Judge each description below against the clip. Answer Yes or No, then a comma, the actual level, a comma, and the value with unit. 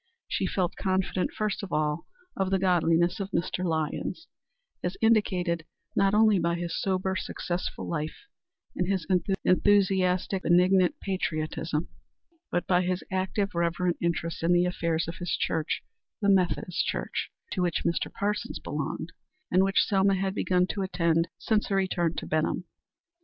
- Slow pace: No, average, 150 wpm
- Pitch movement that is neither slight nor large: No, narrow, 2.2 semitones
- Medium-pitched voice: Yes, medium, 180 Hz